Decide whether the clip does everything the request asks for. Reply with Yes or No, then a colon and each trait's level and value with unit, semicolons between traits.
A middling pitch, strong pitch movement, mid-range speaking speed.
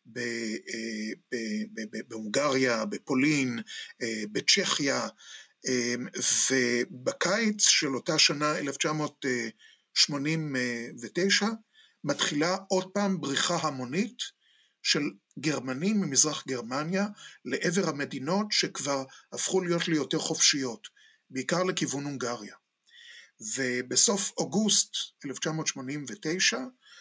No: medium, 150 Hz; wide, 6.8 semitones; slow, 65 wpm